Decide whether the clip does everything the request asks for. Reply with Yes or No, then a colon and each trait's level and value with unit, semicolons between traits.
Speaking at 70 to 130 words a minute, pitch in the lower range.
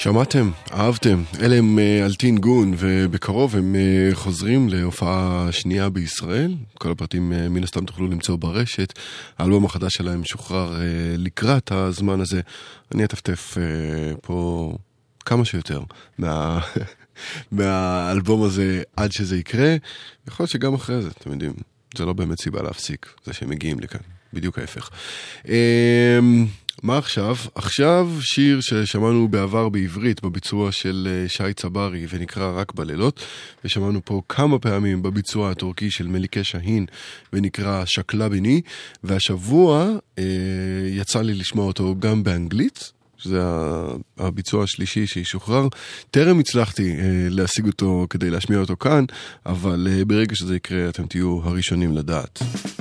Yes: average, 125 wpm; very low, 95 Hz